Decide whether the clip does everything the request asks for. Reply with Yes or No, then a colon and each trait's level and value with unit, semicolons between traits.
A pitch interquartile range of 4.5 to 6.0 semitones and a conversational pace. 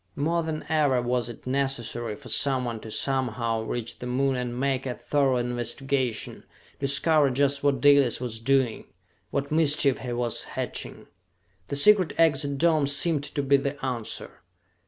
No: average, 2.7 semitones; average, 155 wpm